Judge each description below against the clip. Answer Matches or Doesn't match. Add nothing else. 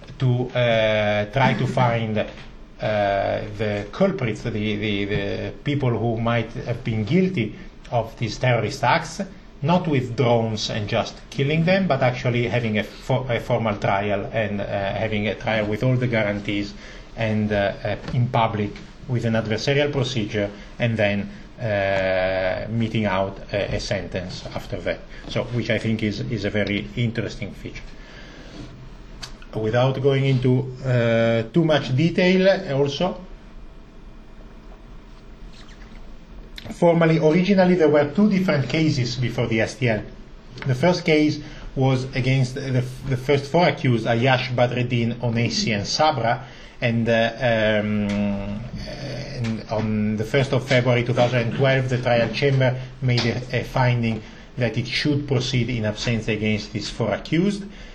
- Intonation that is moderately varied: Matches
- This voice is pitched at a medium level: Doesn't match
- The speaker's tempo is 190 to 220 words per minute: Doesn't match